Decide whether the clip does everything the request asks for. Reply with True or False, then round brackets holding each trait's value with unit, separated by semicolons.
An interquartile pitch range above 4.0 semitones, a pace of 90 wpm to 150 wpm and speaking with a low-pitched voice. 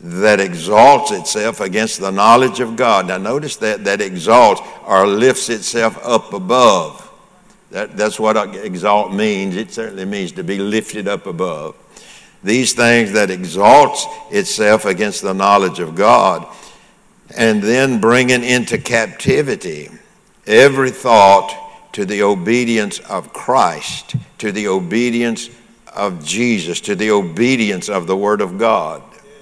False (3.7 semitones; 135 wpm; 115 Hz)